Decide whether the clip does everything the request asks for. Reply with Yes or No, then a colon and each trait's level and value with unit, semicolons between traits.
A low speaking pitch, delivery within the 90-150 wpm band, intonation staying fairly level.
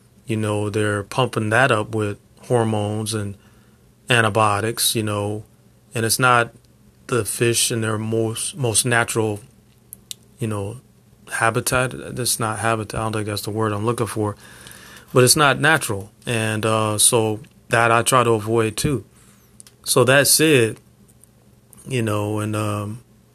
Yes: low, 110 Hz; average, 145 wpm; narrow, 1.7 semitones